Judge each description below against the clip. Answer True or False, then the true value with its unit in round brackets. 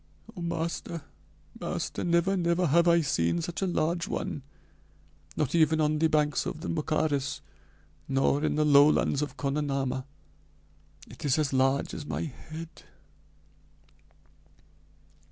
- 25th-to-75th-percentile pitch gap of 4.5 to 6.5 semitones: False (3.0 semitones)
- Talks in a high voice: False (155 Hz)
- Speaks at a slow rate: True (125 wpm)